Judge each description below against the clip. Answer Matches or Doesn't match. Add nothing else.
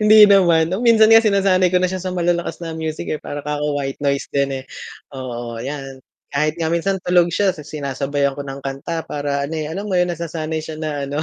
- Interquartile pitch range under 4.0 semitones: Doesn't match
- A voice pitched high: Doesn't match